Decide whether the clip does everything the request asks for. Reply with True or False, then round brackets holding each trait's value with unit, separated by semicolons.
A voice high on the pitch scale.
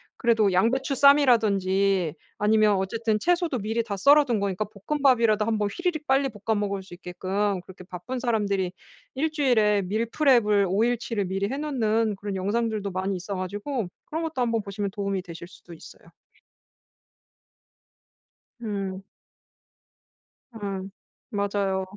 True (210 Hz)